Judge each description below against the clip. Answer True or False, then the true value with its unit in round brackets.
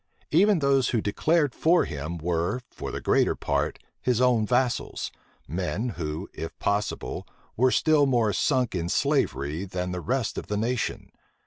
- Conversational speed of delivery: True (155 wpm)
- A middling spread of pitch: False (6.7 semitones)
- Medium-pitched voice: False (115 Hz)